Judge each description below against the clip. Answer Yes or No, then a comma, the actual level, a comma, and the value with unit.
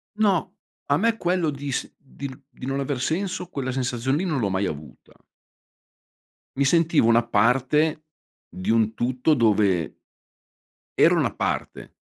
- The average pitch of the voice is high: No, low, 135 Hz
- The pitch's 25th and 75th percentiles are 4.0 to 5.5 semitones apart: Yes, average, 5.2 semitones